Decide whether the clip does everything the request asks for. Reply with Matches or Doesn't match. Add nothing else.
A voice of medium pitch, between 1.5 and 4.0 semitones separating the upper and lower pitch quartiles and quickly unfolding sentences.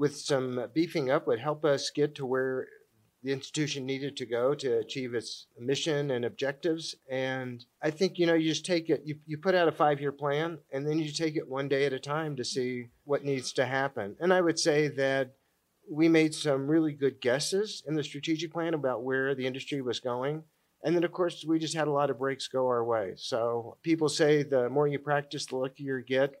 Matches